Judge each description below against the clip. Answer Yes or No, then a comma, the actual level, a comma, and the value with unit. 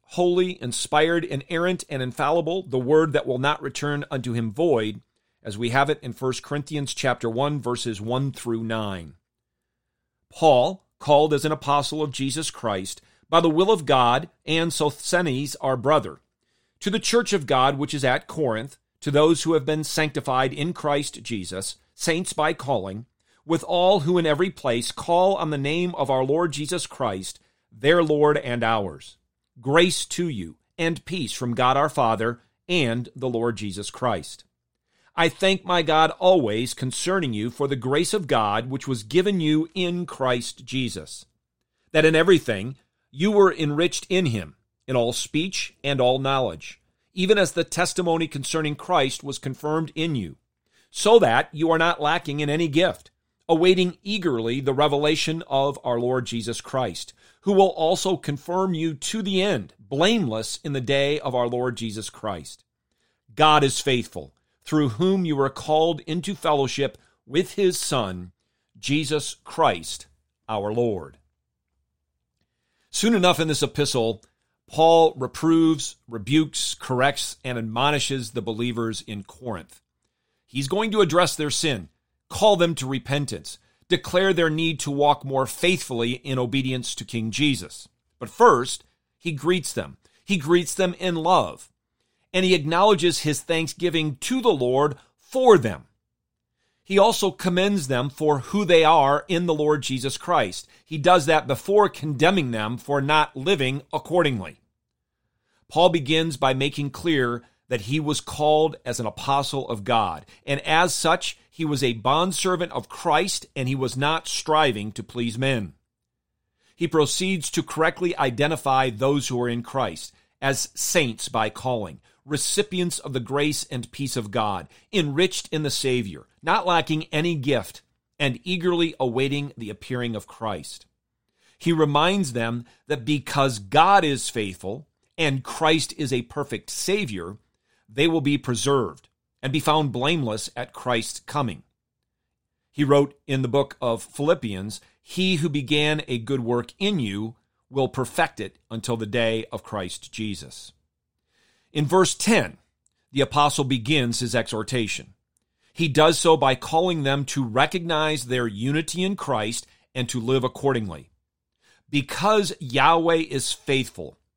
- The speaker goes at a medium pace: Yes, average, 155 wpm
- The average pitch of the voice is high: No, medium, 140 Hz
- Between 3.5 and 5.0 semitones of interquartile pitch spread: No, wide, 5.4 semitones